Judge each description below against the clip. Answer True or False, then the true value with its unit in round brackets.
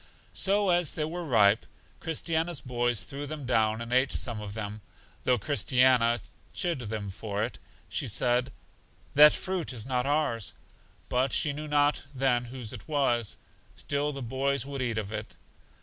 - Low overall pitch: True (130 Hz)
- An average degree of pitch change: True (4.1 semitones)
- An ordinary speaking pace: True (165 wpm)